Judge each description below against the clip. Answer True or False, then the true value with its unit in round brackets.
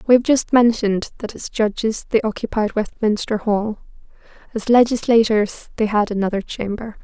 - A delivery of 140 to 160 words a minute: True (145 wpm)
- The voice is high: True (220 Hz)